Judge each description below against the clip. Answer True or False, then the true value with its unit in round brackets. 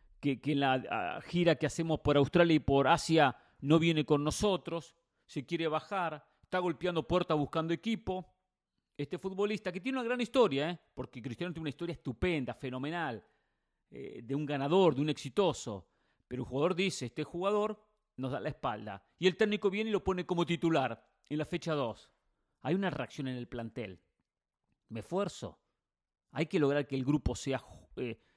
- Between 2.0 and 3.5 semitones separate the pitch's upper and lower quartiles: False (4.7 semitones)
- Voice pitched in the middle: True (155 Hz)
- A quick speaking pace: False (180 wpm)